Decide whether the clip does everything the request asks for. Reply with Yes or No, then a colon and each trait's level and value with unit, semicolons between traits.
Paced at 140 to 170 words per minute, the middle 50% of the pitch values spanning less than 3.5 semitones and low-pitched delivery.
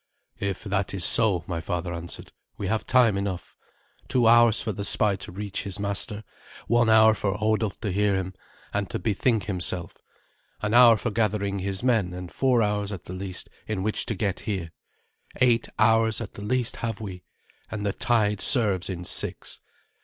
No: average, 185 wpm; average, 2.8 semitones; low, 105 Hz